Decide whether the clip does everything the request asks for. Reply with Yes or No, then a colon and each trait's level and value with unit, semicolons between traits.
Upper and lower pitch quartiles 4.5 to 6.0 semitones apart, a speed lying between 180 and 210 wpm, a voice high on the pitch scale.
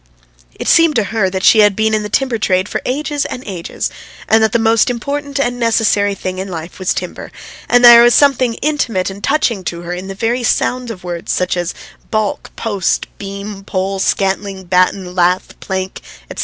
No: average, 4.1 semitones; average, 195 wpm; high, 205 Hz